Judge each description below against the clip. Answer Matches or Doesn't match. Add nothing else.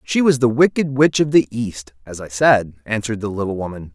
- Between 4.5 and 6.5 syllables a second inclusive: Matches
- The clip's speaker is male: Matches